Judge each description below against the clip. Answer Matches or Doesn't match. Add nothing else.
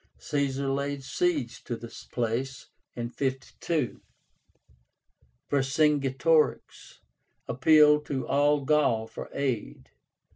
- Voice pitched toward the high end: Doesn't match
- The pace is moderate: Doesn't match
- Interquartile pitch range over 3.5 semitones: Doesn't match